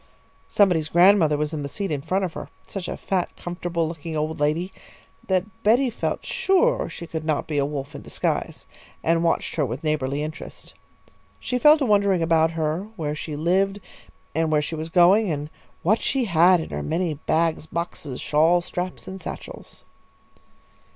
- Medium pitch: Yes, medium, 165 Hz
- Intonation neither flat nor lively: Yes, average, 3.6 semitones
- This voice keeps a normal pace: Yes, average, 180 wpm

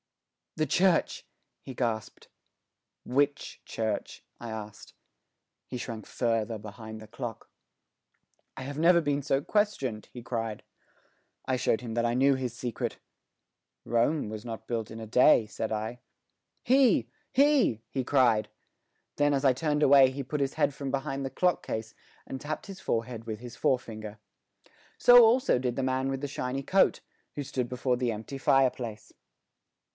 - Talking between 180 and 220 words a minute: No, average, 160 wpm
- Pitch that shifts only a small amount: No, average, 3.8 semitones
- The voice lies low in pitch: Yes, low, 125 Hz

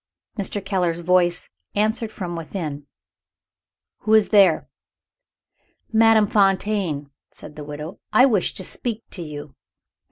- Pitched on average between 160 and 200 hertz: Yes, high, 190 Hz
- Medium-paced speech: No, slow, 120 wpm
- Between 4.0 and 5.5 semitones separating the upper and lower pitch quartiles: Yes, average, 4.6 semitones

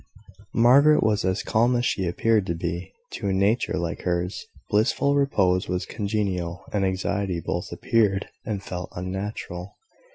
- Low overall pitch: Yes, very low, 95 Hz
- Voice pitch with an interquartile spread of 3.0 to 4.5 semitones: Yes, average, 3.3 semitones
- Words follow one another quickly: No, average, 150 wpm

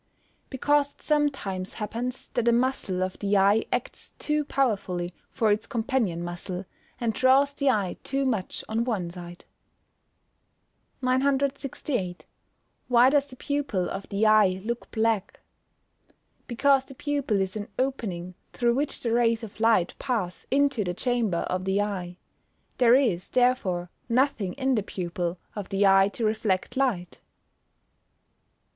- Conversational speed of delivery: Yes, average, 145 wpm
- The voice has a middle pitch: No, high, 225 Hz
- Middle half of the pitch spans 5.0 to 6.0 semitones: Yes, wide, 5.5 semitones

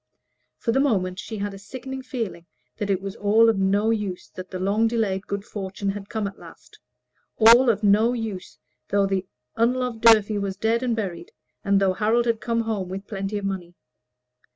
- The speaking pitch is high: Yes, high, 205 Hz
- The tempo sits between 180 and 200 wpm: Yes, average, 190 wpm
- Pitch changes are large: No, average, 2.7 semitones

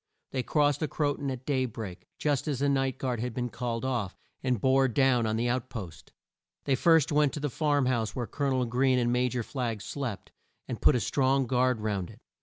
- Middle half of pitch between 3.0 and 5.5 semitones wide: No, narrow, 2.6 semitones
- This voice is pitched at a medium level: No, low, 130 Hz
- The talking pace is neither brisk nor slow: No, fast, 230 wpm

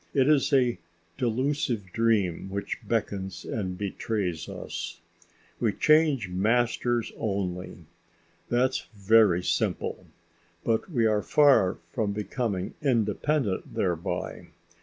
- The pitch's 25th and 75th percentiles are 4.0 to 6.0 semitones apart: Yes, average, 4.4 semitones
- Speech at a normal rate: No, slow, 100 wpm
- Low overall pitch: Yes, low, 110 Hz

